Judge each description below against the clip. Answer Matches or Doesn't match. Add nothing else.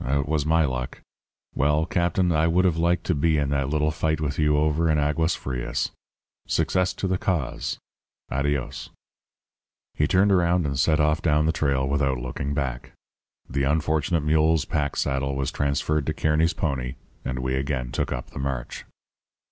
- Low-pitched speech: Matches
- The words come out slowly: Doesn't match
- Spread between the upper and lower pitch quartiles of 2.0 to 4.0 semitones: Matches